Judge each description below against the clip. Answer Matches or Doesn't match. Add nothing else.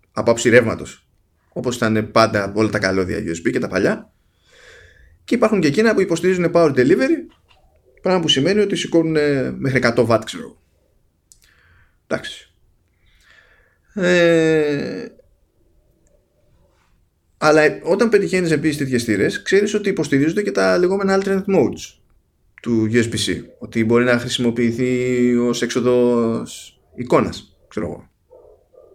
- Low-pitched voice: Matches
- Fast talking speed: Doesn't match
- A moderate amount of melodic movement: Doesn't match